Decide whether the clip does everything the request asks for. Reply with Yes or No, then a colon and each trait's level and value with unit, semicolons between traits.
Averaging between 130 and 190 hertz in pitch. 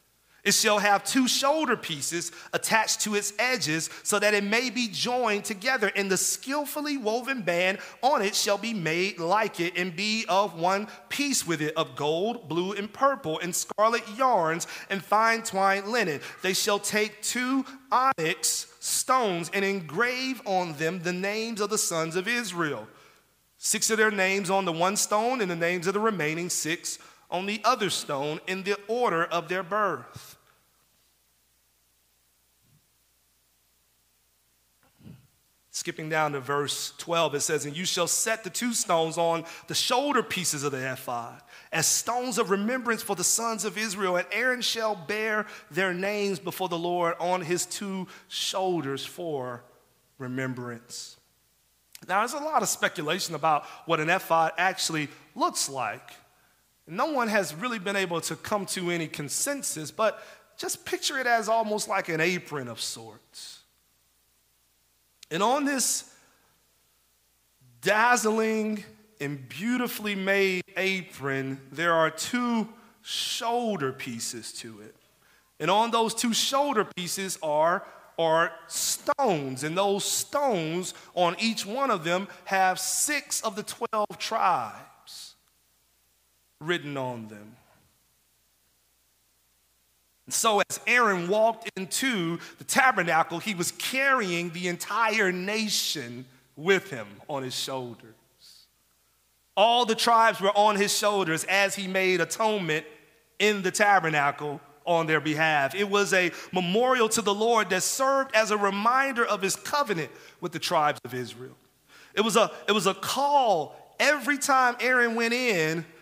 Yes: medium, 185 Hz